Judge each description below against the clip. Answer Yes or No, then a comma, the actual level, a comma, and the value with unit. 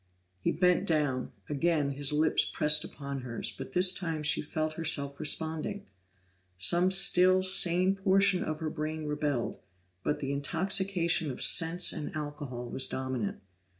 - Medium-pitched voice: Yes, medium, 155 Hz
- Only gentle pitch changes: No, average, 4.0 semitones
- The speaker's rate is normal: Yes, average, 145 wpm